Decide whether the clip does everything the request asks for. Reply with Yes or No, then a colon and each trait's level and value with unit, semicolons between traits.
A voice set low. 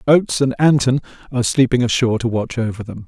Yes: low, 125 Hz